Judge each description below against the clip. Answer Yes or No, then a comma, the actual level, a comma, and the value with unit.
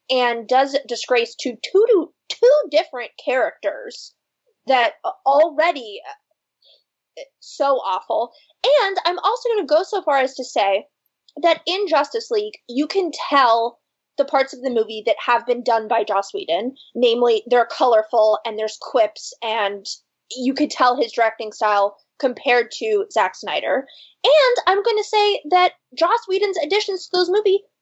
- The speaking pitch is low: No, very high, 285 Hz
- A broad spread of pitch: Yes, wide, 8.0 semitones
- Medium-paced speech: Yes, average, 155 wpm